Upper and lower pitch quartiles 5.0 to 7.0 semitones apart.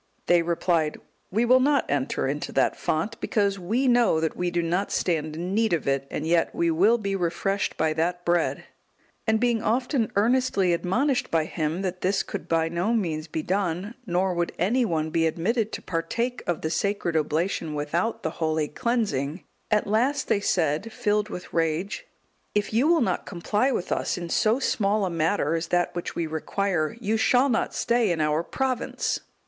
Yes: average, 5.3 semitones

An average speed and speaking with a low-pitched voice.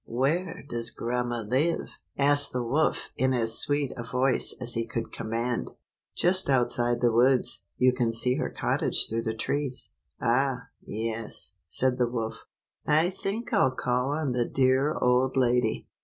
Yes: average, 155 wpm; low, 125 Hz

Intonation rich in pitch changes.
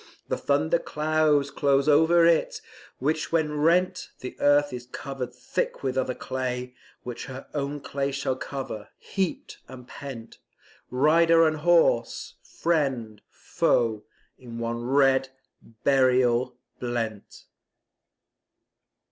No: average, 3.5 semitones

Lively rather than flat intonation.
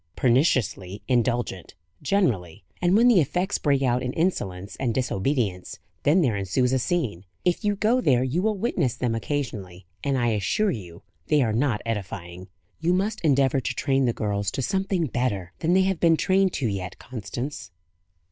Yes: wide, 8.7 semitones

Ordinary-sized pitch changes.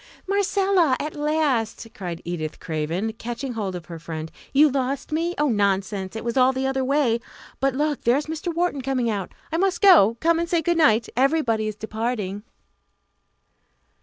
No: wide, 6.3 semitones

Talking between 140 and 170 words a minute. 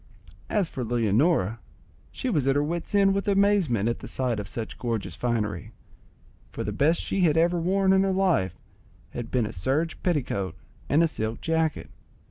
No: average, 185 wpm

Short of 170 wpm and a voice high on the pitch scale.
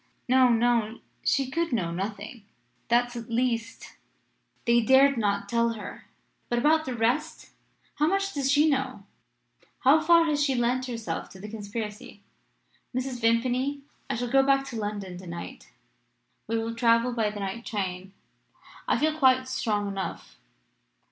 Yes: average, 155 wpm; high, 235 Hz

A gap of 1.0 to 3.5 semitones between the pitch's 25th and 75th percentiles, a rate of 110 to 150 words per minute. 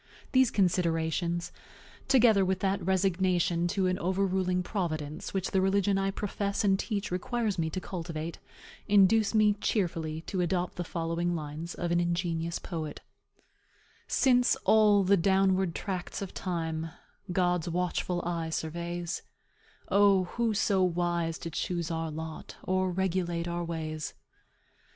Yes: narrow, 2.5 semitones; slow, 135 wpm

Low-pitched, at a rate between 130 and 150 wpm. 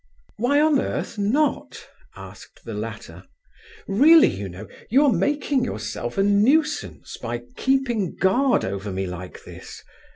No: high, 230 Hz; slow, 135 wpm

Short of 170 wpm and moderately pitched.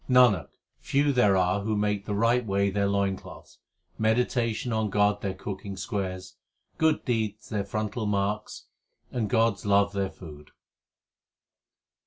No: average, 145 wpm; low, 105 Hz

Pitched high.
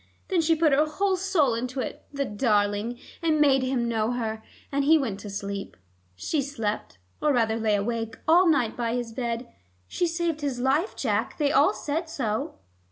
Yes: very high, 255 Hz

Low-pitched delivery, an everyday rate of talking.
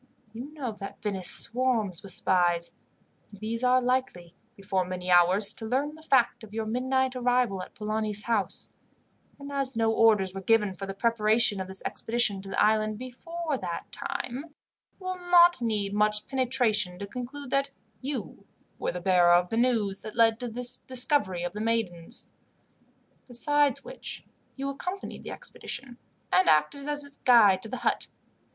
No: high, 225 Hz; average, 170 wpm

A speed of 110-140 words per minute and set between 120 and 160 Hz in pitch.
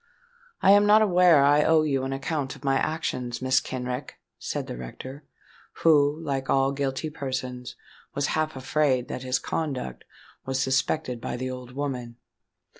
No: average, 165 wpm; low, 135 Hz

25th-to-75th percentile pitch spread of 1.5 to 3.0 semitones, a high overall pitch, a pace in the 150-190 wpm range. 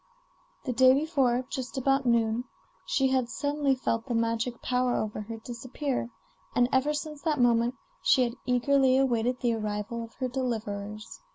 Yes: narrow, 2.5 semitones; very high, 250 Hz; average, 160 wpm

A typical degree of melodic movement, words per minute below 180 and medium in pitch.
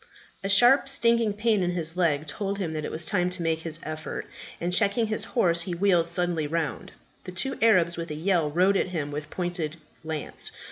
No: average, 3.8 semitones; fast, 205 wpm; medium, 175 Hz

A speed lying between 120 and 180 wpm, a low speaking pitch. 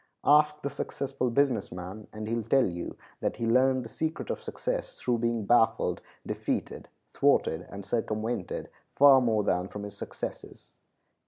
Yes: average, 160 wpm; low, 115 Hz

